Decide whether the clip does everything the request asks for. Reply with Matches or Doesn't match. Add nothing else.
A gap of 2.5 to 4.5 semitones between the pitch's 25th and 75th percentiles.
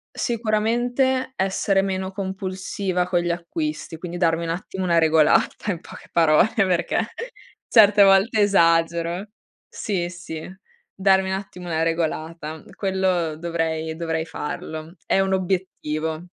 Matches